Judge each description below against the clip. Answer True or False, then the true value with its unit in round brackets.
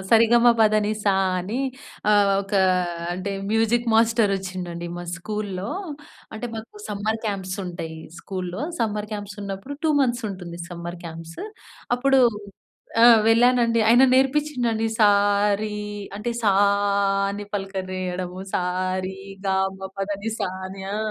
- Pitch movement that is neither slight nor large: True (3.4 semitones)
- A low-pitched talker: False (205 Hz)